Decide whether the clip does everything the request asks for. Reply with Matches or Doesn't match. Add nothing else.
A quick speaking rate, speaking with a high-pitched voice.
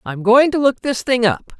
Matches